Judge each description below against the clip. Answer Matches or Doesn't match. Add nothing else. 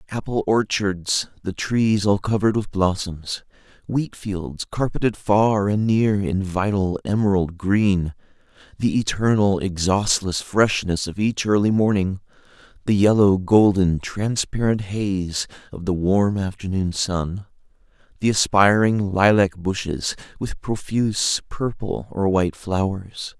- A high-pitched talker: Doesn't match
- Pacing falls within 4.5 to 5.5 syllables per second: Doesn't match